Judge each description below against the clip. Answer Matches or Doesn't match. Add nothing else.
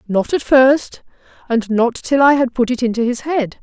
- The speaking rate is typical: Doesn't match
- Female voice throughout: Matches